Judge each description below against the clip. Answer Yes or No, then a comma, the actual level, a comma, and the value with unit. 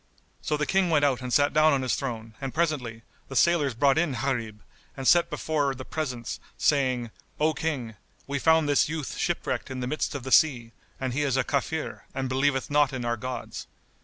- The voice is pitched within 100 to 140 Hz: Yes, low, 135 Hz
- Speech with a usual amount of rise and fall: Yes, average, 3.1 semitones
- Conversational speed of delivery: No, fast, 210 wpm